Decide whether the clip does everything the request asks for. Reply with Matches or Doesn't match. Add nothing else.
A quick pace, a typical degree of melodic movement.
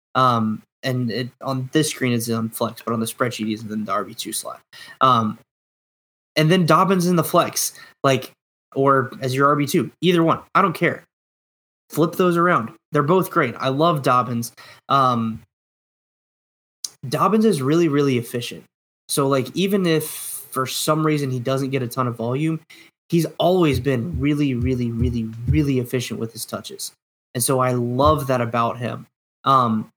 Doesn't match